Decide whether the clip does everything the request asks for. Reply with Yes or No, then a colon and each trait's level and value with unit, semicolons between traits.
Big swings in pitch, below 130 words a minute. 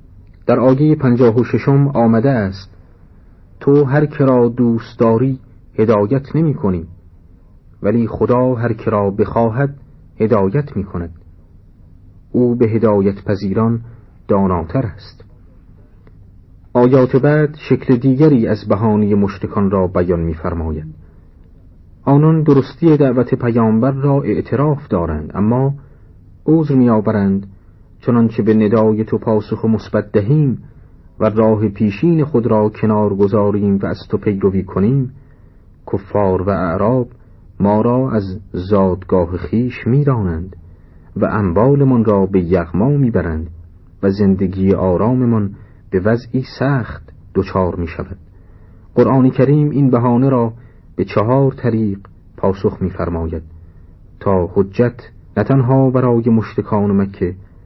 No: average, 4.7 semitones; average, 120 wpm